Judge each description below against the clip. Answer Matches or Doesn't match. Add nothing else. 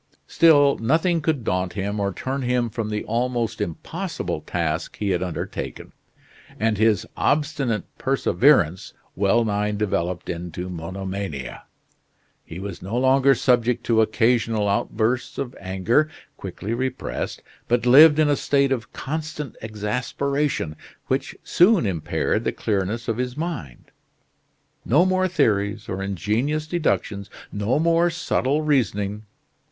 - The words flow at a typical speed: Doesn't match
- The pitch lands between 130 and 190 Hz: Doesn't match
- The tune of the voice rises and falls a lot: Matches